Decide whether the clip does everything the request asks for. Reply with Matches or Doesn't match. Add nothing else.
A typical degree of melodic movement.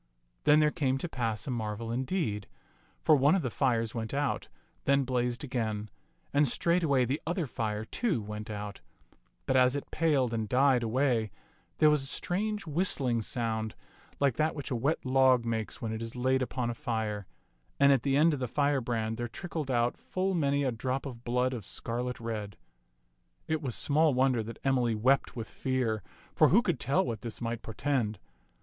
Matches